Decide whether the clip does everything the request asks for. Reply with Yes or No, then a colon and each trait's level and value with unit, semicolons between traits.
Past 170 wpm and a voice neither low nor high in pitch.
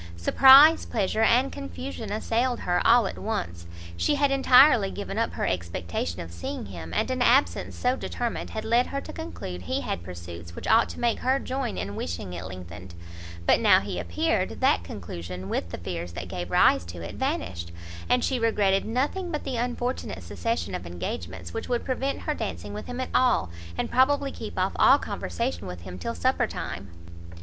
Yes: average, 190 wpm; medium, 175 Hz